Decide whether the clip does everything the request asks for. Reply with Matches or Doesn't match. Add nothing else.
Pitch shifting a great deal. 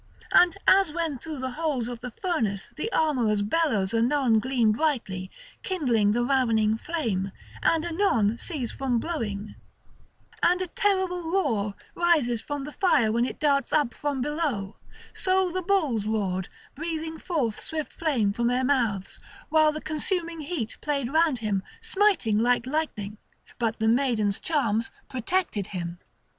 Matches